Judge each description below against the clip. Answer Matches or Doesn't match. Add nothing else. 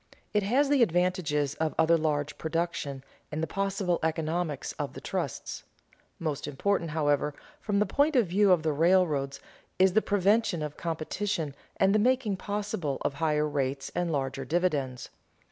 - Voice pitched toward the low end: Doesn't match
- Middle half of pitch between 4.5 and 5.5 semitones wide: Matches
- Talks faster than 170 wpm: Doesn't match